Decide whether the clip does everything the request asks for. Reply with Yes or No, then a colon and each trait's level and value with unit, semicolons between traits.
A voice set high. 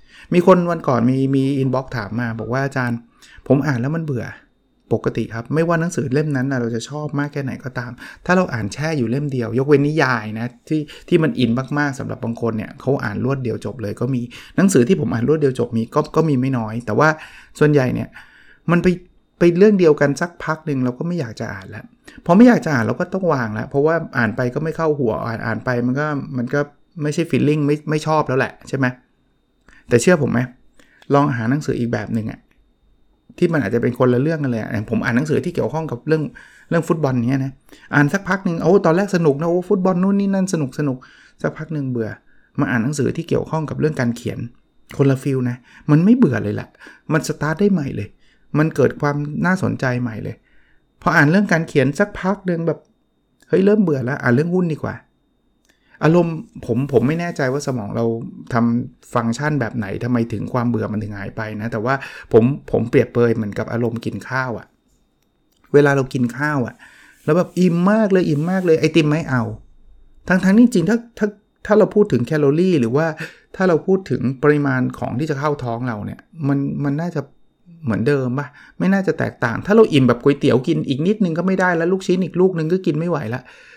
No: medium, 140 Hz